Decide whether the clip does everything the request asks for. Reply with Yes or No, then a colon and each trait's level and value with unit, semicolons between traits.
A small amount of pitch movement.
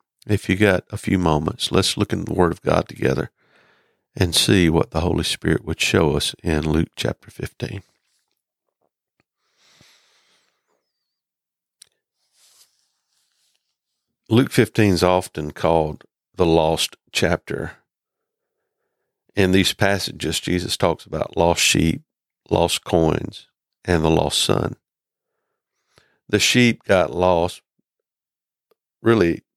No: wide, 5.5 semitones